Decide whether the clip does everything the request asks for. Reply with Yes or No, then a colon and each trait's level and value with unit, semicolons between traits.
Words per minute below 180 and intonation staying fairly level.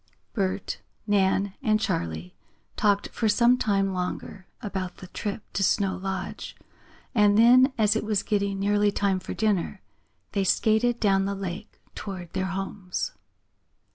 Yes: average, 140 wpm; narrow, 2.1 semitones